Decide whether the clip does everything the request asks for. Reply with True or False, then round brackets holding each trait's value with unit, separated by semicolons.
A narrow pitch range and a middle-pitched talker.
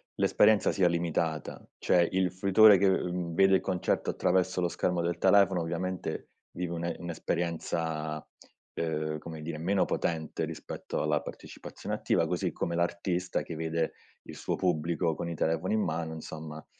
False (2.2 semitones; 85 Hz)